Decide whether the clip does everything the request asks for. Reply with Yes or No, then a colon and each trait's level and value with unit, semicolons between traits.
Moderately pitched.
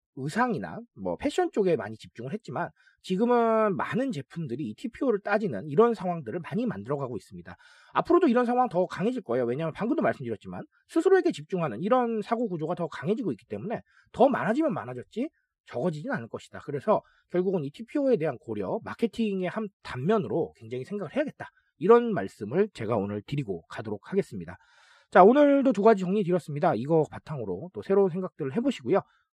No: high, 205 Hz